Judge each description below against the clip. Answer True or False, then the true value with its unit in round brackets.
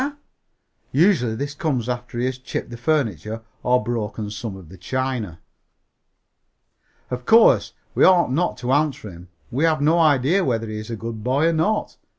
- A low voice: True (125 Hz)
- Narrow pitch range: False (5.3 semitones)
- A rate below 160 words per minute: False (170 wpm)